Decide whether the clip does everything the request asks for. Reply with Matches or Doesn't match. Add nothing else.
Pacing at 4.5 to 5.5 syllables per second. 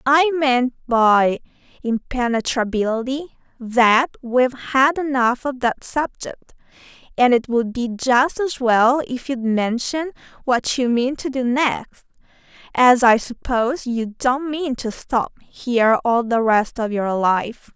Doesn't match